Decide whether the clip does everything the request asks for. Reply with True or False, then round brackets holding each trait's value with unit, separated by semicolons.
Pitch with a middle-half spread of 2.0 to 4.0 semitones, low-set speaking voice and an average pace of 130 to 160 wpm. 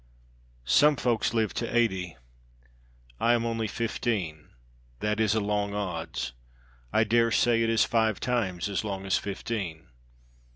True (3.3 semitones; 110 Hz; 140 wpm)